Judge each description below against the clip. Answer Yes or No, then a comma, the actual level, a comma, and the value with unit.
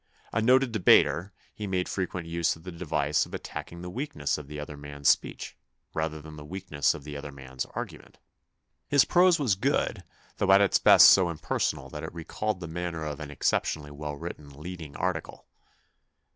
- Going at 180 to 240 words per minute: Yes, average, 185 wpm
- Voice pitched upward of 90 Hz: No, very low, 80 Hz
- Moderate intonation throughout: Yes, average, 4.1 semitones